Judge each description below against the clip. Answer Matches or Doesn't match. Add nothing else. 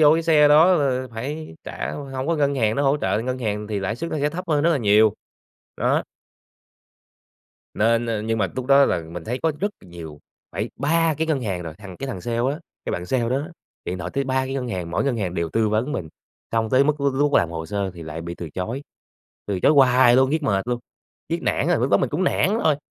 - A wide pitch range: Matches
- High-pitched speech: Doesn't match